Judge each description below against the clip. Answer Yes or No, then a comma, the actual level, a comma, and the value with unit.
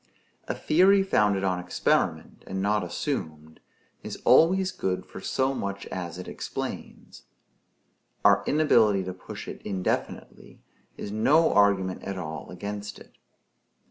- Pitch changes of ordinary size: No, wide, 6.1 semitones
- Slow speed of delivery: Yes, slow, 130 wpm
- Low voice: Yes, low, 100 Hz